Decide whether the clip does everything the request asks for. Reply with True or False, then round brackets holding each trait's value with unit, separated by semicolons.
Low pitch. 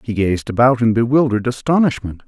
True (120 Hz)